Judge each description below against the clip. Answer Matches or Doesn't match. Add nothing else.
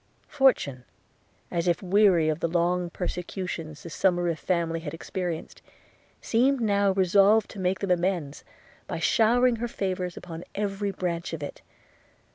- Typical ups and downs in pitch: Matches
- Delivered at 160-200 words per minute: Doesn't match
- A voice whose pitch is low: Doesn't match